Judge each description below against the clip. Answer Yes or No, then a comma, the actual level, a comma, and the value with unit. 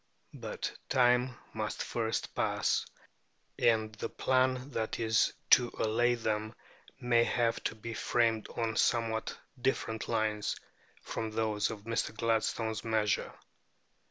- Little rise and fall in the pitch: Yes, narrow, 1.6 semitones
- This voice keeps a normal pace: No, slow, 120 wpm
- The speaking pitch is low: Yes, low, 115 Hz